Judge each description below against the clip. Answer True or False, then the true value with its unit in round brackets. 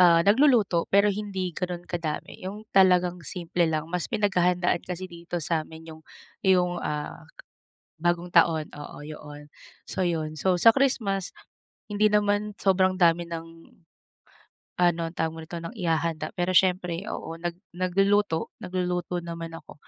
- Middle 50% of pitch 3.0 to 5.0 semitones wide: False (2.4 semitones)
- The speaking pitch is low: False (175 Hz)